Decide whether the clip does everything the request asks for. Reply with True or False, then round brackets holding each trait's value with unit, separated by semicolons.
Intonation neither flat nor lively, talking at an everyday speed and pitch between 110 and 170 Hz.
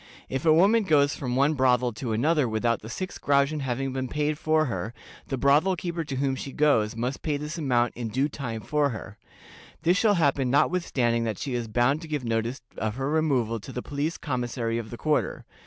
False (4.0 semitones; 210 wpm; 135 Hz)